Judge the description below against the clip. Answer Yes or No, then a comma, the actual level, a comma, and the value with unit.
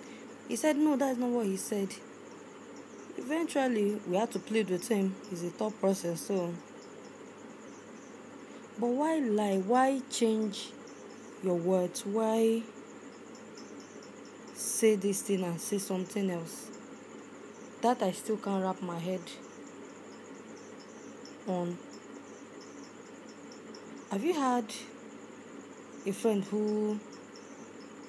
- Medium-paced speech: No, slow, 105 wpm